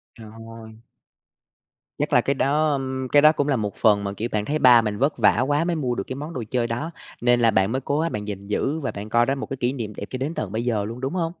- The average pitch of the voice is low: Yes, low, 125 Hz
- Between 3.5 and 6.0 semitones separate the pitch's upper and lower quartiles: Yes, average, 4.4 semitones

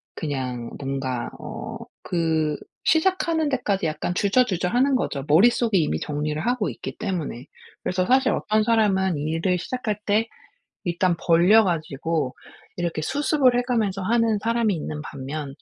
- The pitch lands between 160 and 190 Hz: Yes, medium, 185 Hz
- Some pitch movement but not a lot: No, wide, 7.0 semitones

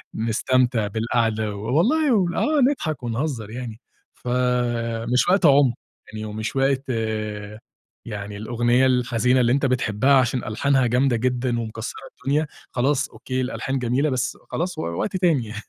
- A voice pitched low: Yes, low, 125 Hz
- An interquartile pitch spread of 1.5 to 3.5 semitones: Yes, average, 3.1 semitones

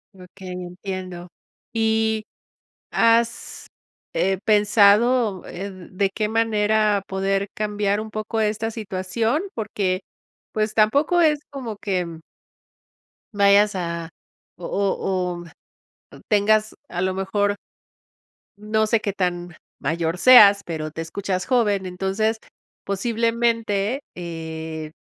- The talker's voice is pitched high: Yes, high, 200 Hz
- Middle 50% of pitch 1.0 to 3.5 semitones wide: Yes, average, 3.0 semitones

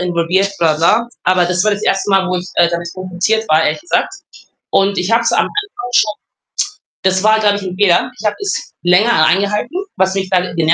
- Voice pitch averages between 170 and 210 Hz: Yes, high, 190 Hz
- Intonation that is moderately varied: Yes, average, 3.1 semitones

